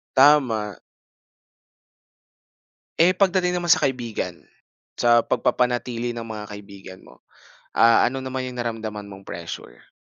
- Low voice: Yes, low, 120 Hz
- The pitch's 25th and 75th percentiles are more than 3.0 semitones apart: Yes, average, 4.0 semitones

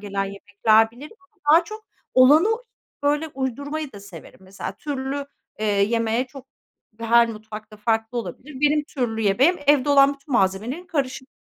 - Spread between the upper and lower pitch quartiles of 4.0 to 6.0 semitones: Yes, average, 5.1 semitones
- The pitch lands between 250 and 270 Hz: Yes, very high, 255 Hz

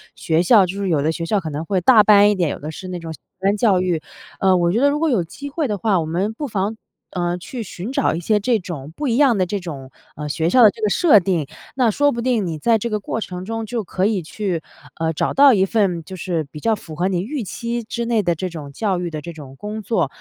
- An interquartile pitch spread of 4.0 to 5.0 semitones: Yes, average, 4.7 semitones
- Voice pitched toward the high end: Yes, high, 195 Hz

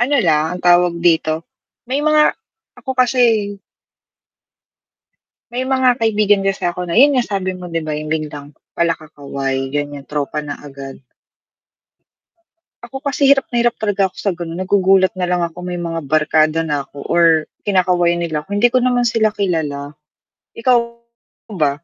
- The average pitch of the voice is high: No, medium, 180 Hz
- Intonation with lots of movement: Yes, wide, 6.5 semitones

